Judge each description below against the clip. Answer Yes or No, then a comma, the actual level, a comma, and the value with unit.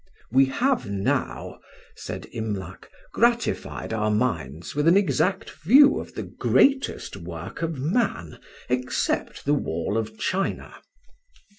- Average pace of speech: No, slow, 120 wpm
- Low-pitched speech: Yes, low, 130 Hz